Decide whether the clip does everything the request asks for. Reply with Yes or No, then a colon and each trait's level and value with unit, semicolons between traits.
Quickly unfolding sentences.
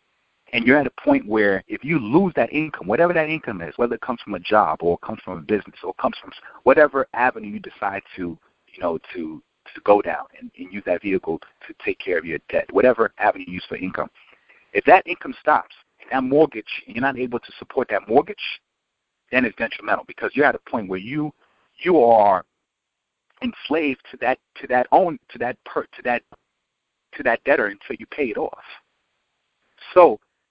Yes: fast, 210 wpm